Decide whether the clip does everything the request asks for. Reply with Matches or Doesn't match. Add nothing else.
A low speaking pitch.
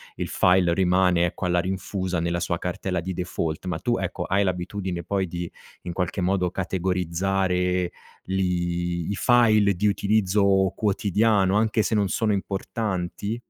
Matches